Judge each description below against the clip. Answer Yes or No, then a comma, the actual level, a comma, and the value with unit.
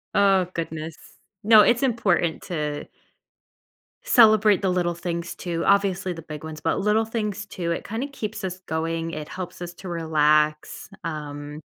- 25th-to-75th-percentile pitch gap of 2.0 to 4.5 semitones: Yes, average, 4.2 semitones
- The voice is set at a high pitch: No, medium, 175 Hz